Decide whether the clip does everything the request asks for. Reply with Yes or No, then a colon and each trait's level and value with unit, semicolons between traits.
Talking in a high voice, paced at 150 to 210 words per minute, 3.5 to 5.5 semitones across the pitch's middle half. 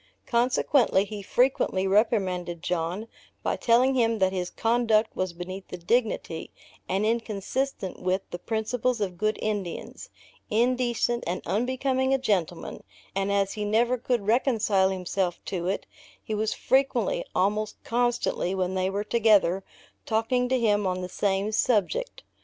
No: high, 210 Hz; average, 140 wpm; average, 4.1 semitones